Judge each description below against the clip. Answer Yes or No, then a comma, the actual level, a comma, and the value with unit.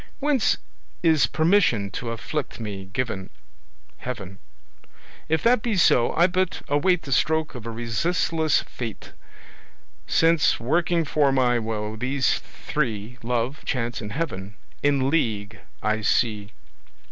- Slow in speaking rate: Yes, slow, 125 wpm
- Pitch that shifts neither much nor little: No, wide, 6.4 semitones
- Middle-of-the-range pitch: No, low, 125 Hz